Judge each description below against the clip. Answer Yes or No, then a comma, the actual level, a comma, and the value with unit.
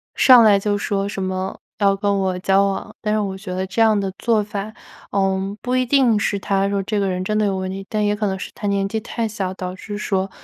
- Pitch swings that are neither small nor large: No, narrow, 1.7 semitones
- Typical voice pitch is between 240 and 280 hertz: No, high, 200 Hz